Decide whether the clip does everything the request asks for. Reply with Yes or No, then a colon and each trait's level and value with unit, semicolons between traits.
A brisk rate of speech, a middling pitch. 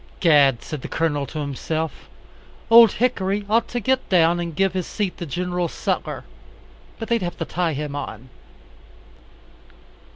No: average, 155 wpm; medium, 175 Hz